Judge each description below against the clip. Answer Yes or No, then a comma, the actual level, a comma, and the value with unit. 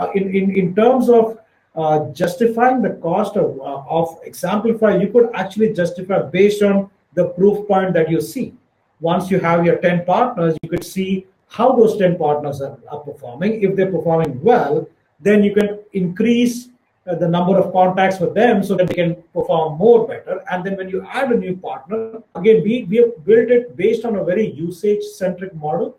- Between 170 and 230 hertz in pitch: Yes, high, 190 Hz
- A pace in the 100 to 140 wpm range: No, average, 200 wpm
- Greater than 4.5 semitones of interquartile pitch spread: No, average, 4.2 semitones